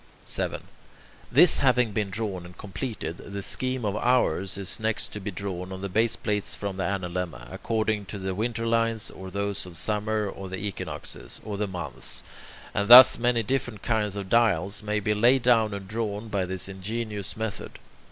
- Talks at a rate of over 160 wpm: Yes, average, 180 wpm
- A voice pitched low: Yes, low, 105 Hz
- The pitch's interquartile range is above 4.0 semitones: No, average, 2.8 semitones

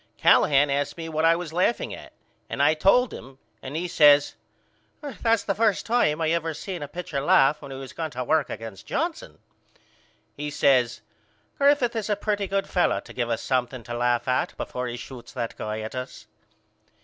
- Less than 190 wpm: No, average, 195 wpm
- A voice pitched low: No, medium, 150 Hz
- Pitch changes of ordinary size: No, wide, 6.4 semitones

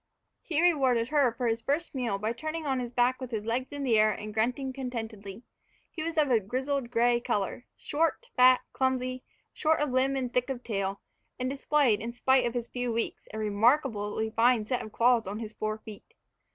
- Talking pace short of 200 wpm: No, fast, 205 wpm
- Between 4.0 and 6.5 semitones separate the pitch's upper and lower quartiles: No, average, 3.2 semitones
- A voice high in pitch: Yes, high, 245 Hz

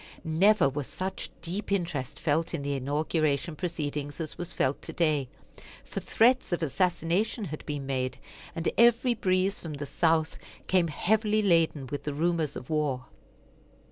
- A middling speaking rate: Yes, average, 150 wpm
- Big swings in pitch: No, average, 4.3 semitones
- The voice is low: No, medium, 160 Hz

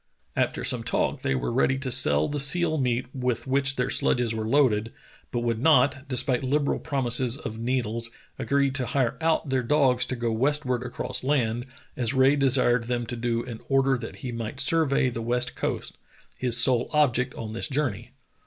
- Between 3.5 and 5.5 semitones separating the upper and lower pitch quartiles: No, narrow, 2.6 semitones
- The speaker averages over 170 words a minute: Yes, average, 190 wpm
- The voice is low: Yes, low, 125 Hz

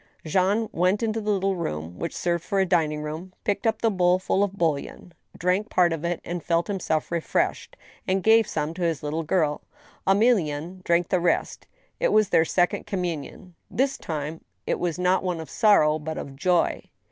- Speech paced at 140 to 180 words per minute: No, average, 190 wpm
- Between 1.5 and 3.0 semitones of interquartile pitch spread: No, average, 3.4 semitones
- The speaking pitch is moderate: Yes, medium, 180 Hz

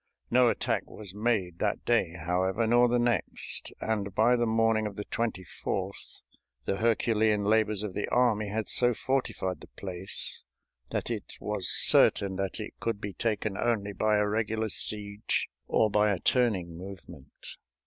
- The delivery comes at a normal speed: Yes, average, 160 wpm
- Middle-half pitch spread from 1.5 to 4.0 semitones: Yes, narrow, 2.5 semitones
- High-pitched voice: No, low, 105 Hz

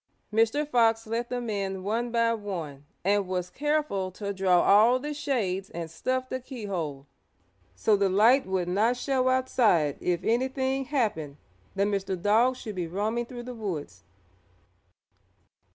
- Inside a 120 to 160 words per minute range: Yes, average, 150 wpm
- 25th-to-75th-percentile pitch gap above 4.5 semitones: Yes, average, 4.9 semitones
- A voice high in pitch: Yes, high, 215 Hz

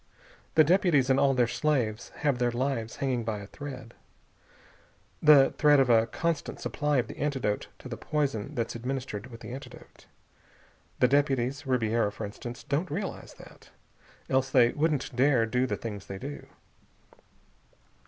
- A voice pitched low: Yes, low, 130 Hz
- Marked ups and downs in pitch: No, average, 3.6 semitones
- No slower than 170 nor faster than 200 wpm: No, average, 155 wpm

